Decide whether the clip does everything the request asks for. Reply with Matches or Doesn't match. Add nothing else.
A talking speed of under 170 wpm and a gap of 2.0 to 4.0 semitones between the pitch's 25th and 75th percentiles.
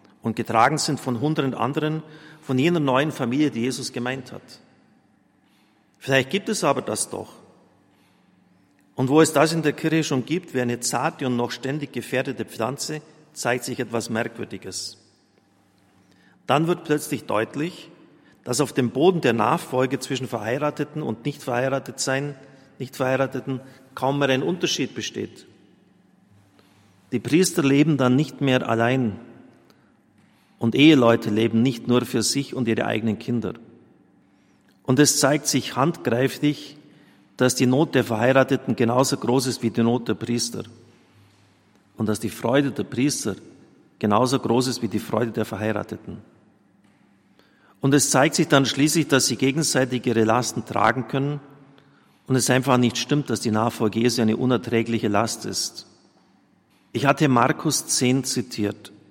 Matches